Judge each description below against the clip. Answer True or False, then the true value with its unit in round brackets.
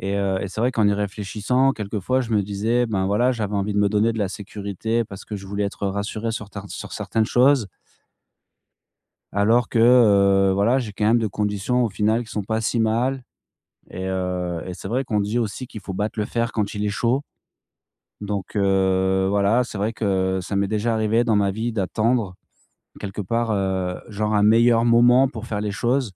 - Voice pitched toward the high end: False (105 Hz)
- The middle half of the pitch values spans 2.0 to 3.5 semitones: True (2.7 semitones)